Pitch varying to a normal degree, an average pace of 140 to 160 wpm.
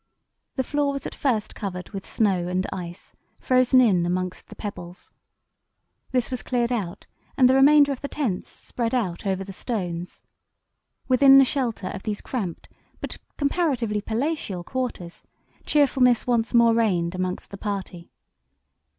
No: wide, 5.9 semitones; average, 150 wpm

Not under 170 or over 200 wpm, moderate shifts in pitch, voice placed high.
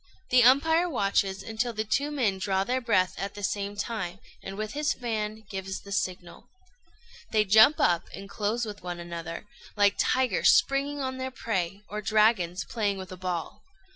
Yes: average, 175 wpm; average, 3.9 semitones; high, 210 Hz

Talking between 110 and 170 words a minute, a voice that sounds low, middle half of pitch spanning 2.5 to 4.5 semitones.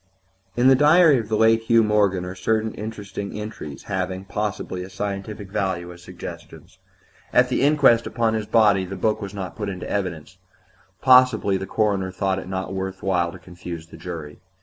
No: average, 185 wpm; low, 100 Hz; average, 3.0 semitones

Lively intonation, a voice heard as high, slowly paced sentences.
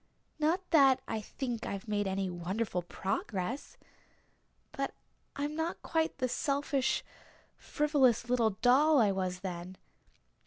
Yes: wide, 6.9 semitones; high, 240 Hz; slow, 120 wpm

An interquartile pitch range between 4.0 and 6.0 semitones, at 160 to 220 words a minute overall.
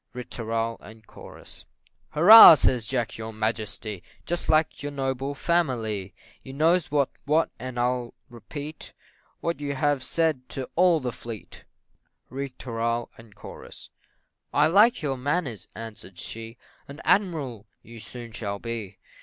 No: average, 4.7 semitones; slow, 135 wpm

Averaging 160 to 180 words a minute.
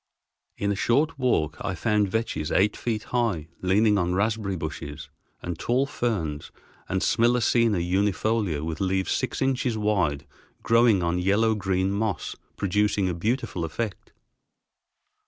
No: slow, 135 wpm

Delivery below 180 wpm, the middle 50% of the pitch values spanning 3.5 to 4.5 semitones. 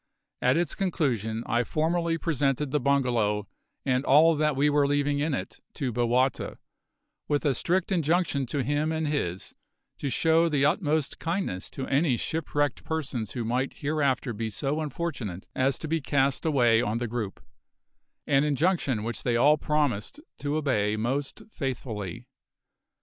Yes: average, 155 wpm; average, 4.1 semitones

